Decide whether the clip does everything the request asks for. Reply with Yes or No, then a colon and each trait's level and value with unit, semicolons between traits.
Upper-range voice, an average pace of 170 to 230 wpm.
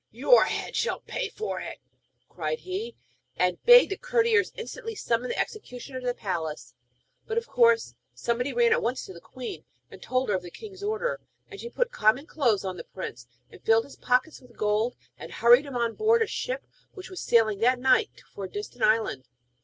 Yes: very high, 255 Hz; average, 200 wpm